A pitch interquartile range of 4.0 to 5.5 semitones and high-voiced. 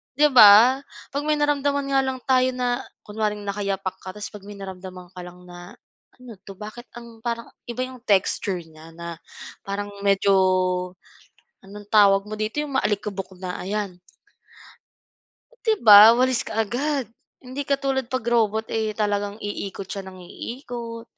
Yes: average, 4.3 semitones; high, 210 Hz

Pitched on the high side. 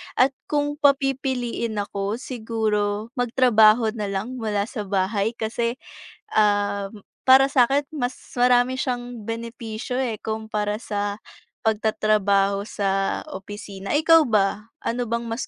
Yes: high, 225 Hz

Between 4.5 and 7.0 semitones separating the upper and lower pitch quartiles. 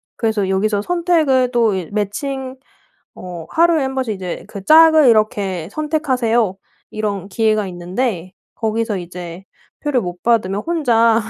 Yes: wide, 5.5 semitones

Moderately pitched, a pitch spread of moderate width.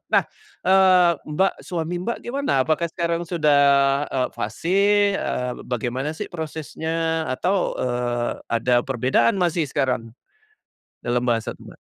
No: medium, 155 Hz; wide, 5.7 semitones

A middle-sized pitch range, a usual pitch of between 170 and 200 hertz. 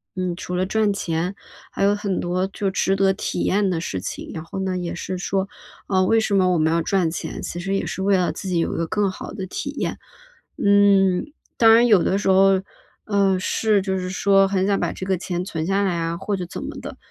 No: narrow, 1.9 semitones; high, 190 Hz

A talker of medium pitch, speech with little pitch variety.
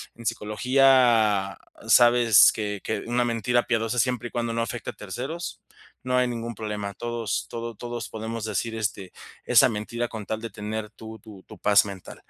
No: low, 115 Hz; narrow, 2.1 semitones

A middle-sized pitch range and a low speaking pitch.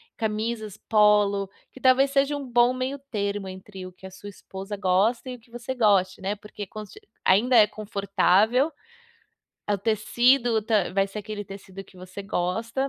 No: average, 3.4 semitones; high, 210 Hz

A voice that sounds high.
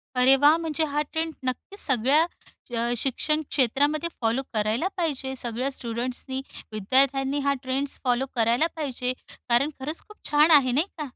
Yes: very high, 270 Hz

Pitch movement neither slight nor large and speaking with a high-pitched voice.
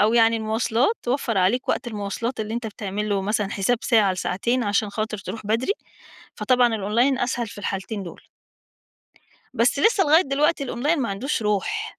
Yes: average, 3.7 semitones; high, 225 Hz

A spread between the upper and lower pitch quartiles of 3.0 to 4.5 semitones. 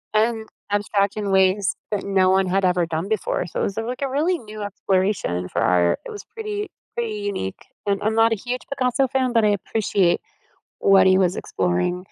Yes: average, 3.7 semitones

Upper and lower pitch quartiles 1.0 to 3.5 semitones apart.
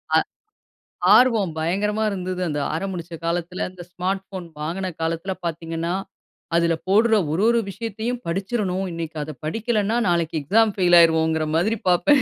No: average, 4.0 semitones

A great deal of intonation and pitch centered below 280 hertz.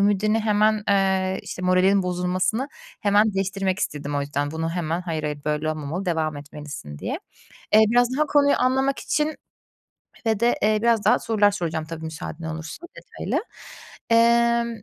Yes: wide, 5.8 semitones; high, 190 Hz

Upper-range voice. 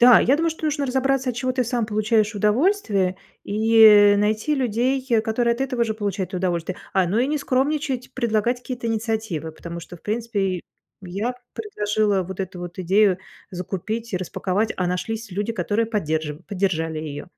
Yes: high, 215 Hz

